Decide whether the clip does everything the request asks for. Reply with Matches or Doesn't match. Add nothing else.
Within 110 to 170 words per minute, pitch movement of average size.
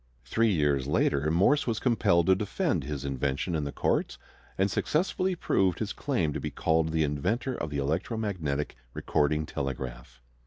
Doesn't match